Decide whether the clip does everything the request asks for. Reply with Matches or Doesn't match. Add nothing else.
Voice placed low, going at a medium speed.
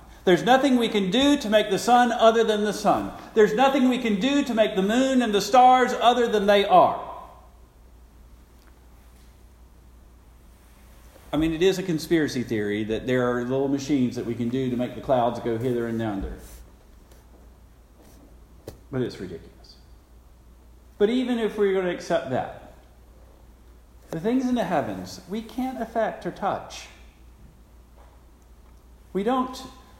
Matches